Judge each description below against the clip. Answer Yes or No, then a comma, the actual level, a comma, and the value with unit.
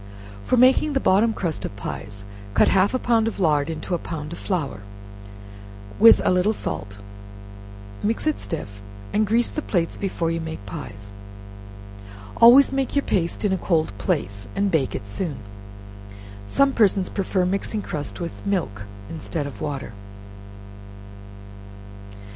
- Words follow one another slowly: No, average, 150 wpm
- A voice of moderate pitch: Yes, medium, 175 Hz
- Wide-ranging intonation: Yes, wide, 7.0 semitones